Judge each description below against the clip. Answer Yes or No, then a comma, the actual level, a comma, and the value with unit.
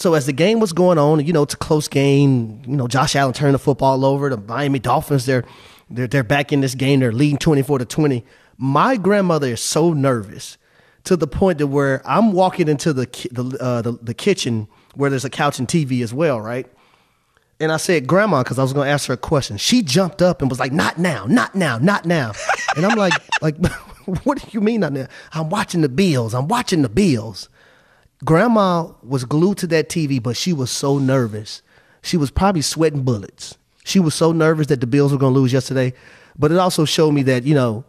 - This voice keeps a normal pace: No, fast, 225 wpm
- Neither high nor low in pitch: Yes, medium, 145 Hz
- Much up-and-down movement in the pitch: No, average, 4.1 semitones